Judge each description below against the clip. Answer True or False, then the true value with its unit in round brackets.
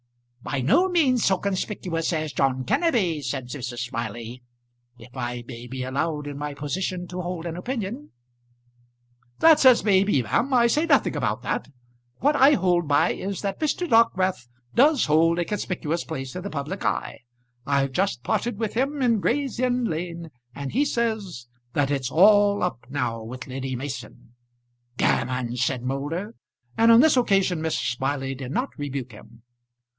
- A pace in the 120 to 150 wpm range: False (165 wpm)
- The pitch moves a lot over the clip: True (8.6 semitones)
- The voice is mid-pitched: True (165 Hz)